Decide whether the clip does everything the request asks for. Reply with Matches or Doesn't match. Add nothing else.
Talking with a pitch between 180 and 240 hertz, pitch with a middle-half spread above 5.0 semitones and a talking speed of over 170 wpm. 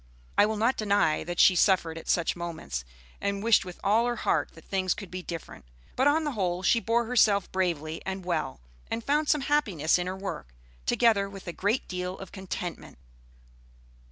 Doesn't match